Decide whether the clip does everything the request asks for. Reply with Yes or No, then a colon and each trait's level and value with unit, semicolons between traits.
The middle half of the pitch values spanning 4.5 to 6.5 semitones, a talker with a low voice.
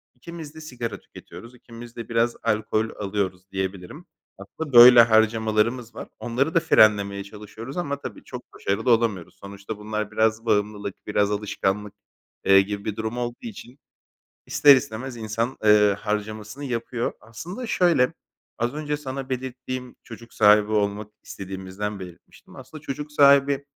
No: average, 3.7 semitones; low, 110 Hz